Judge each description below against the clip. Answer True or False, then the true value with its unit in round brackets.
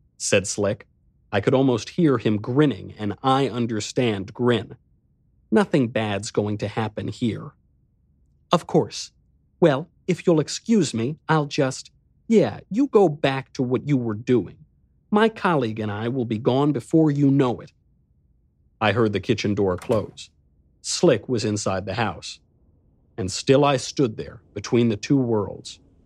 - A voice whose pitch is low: True (120 Hz)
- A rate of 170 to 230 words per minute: False (155 wpm)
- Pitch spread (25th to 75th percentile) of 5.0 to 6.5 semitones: True (5.3 semitones)